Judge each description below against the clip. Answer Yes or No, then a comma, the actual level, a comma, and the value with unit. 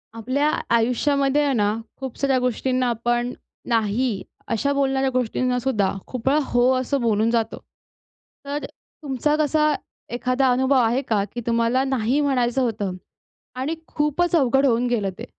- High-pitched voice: Yes, very high, 255 Hz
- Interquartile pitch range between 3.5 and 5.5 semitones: No, average, 2.8 semitones